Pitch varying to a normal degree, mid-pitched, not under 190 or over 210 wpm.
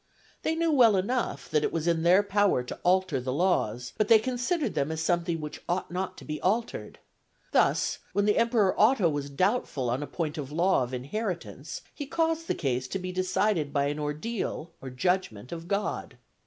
No: wide, 6.2 semitones; medium, 180 Hz; average, 200 wpm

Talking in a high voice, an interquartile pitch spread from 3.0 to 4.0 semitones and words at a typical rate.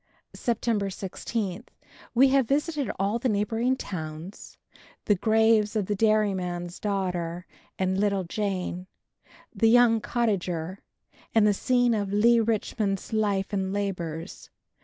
No: high, 205 Hz; average, 3.3 semitones; slow, 120 wpm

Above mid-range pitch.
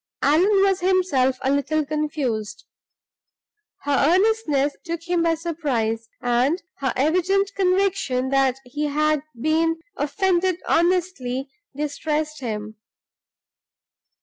Yes: very high, 305 Hz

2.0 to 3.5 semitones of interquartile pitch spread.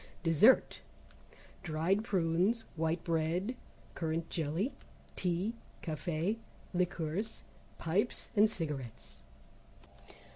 No: average, 4.1 semitones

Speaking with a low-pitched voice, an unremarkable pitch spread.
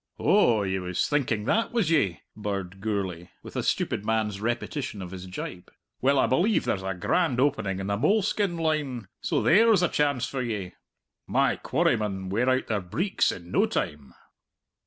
No: low, 110 Hz; wide, 7.5 semitones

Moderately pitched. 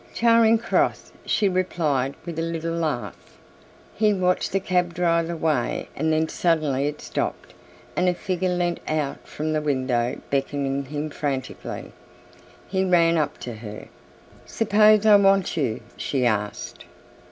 Yes: medium, 165 Hz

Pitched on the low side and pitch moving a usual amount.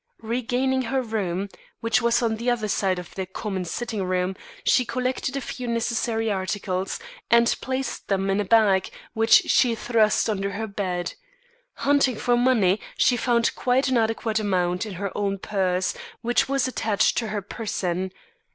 No: high, 220 Hz; average, 3.9 semitones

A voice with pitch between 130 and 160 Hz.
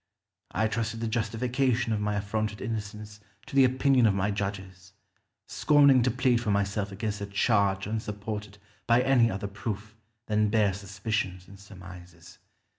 No: low, 105 Hz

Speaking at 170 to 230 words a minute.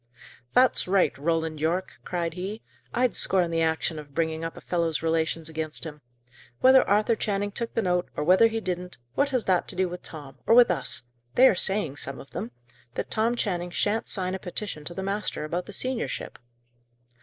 Yes: average, 200 wpm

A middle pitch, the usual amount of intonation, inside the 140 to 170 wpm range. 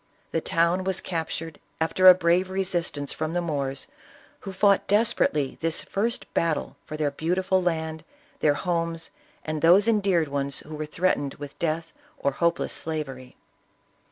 Yes: medium, 165 Hz; average, 3.2 semitones; average, 155 wpm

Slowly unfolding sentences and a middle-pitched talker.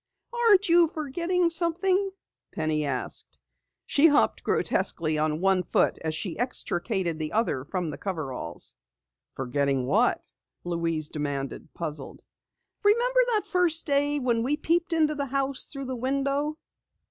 No: slow, 130 wpm; very high, 255 Hz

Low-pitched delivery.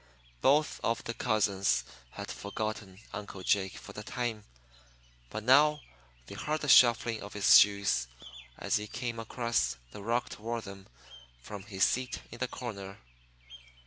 Yes: low, 110 Hz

